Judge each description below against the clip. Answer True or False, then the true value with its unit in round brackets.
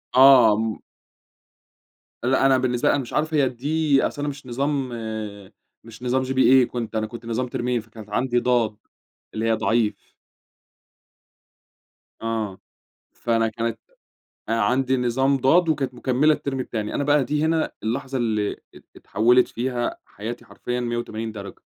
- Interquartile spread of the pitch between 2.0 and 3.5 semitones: True (2.8 semitones)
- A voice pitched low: True (125 Hz)